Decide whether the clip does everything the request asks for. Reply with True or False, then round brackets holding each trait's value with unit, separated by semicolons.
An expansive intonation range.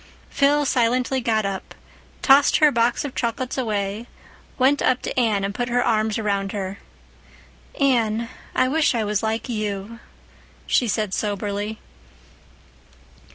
False (3.6 semitones)